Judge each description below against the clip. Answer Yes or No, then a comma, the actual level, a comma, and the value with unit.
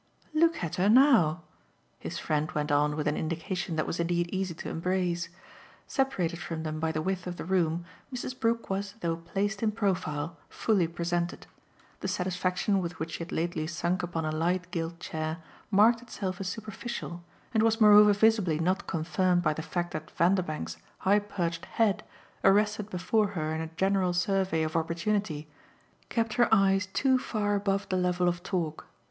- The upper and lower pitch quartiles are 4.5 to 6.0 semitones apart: No, average, 3.6 semitones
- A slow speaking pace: No, average, 175 wpm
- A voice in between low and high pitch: Yes, medium, 180 Hz